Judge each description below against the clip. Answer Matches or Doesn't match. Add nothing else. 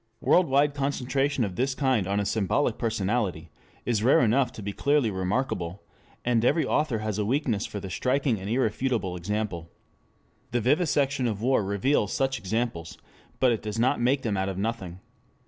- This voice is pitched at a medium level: Doesn't match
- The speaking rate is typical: Matches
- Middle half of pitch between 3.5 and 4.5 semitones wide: Doesn't match